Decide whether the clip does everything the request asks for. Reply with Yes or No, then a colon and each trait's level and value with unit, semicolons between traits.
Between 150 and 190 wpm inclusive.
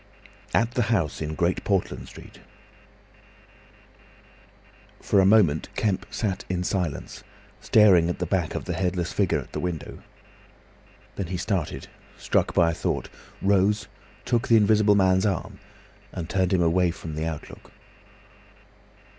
No: average, 140 wpm